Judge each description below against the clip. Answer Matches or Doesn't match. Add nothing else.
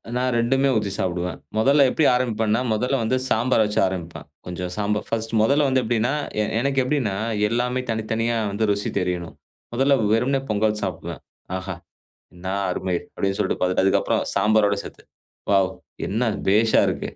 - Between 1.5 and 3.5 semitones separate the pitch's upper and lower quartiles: Doesn't match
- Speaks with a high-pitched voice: Doesn't match